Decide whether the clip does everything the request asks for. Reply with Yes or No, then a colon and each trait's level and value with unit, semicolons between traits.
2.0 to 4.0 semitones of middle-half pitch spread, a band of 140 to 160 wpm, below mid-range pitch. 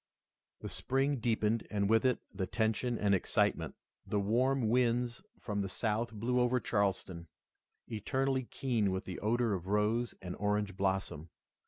Yes: average, 3.5 semitones; average, 150 wpm; low, 110 Hz